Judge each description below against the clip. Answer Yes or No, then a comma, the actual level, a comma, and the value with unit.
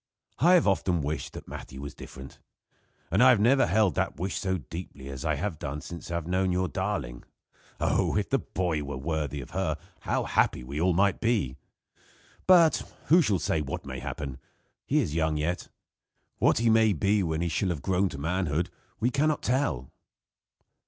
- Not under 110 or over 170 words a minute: No, average, 195 wpm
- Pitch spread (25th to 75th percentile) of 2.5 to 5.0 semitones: No, wide, 5.4 semitones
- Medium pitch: No, very low, 85 Hz